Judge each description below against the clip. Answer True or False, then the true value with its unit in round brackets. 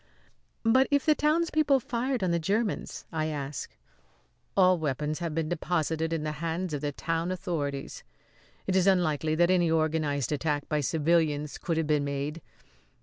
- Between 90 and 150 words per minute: False (160 wpm)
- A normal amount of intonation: True (3.5 semitones)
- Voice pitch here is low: False (160 Hz)